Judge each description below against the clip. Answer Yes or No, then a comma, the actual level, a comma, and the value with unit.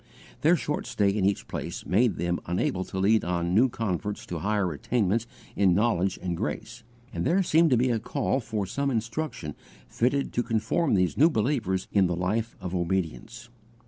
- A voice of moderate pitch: No, low, 105 Hz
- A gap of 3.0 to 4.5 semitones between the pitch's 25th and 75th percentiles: No, average, 4.9 semitones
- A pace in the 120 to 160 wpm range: No, average, 180 wpm